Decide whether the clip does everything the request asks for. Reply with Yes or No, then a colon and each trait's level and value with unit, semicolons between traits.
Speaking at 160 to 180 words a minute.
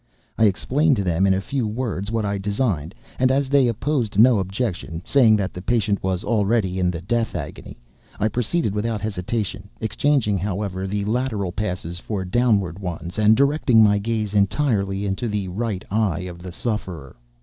Yes: average, 170 wpm